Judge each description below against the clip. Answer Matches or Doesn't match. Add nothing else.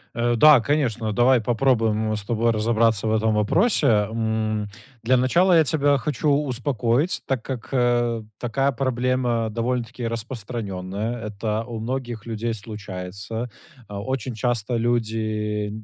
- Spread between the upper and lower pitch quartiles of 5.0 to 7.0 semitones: Doesn't match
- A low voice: Matches